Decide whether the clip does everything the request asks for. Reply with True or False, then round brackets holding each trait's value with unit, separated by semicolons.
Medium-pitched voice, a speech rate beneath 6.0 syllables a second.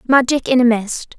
False (245 Hz; 4.9 syllables/s)